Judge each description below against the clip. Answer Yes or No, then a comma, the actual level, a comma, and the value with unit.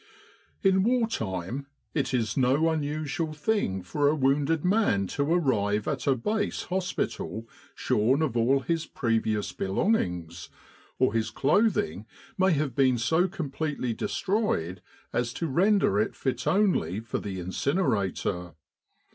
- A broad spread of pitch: Yes, wide, 8.2 semitones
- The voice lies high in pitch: No, low, 135 Hz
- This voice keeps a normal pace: No, slow, 130 wpm